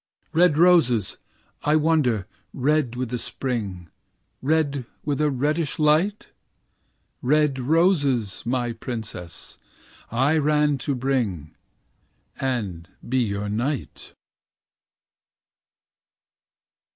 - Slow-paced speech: Yes, slow, 90 wpm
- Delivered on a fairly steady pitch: No, average, 4.6 semitones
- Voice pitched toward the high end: No, low, 130 Hz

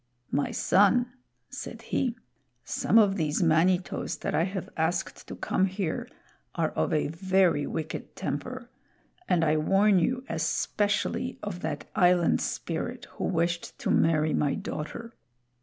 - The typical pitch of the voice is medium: Yes, medium, 180 Hz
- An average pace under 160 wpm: Yes, average, 140 wpm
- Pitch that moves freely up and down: No, average, 4.3 semitones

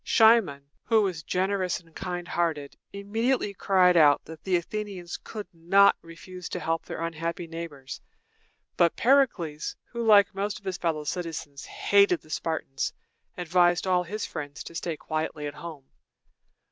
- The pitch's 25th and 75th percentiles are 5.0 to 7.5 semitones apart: No, average, 3.6 semitones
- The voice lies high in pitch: No, medium, 175 Hz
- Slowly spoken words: No, average, 150 wpm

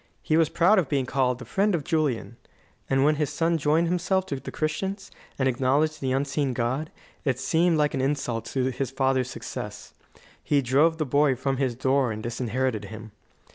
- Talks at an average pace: Yes, average, 190 wpm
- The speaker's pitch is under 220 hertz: Yes, low, 135 Hz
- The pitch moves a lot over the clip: No, average, 3.4 semitones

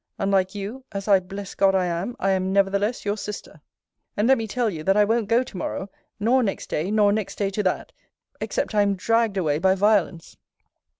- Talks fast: Yes, fast, 215 wpm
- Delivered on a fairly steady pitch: Yes, narrow, 2.1 semitones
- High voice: Yes, high, 200 Hz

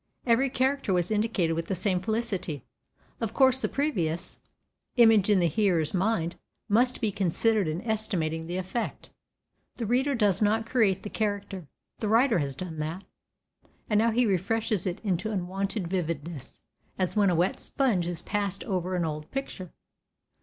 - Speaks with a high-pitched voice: Yes, high, 195 Hz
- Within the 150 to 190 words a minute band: Yes, average, 160 wpm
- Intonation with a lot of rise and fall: No, average, 4.4 semitones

